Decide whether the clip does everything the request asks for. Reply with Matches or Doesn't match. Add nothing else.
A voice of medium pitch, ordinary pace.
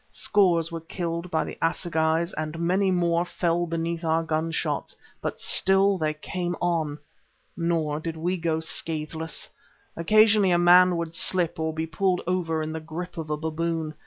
Matches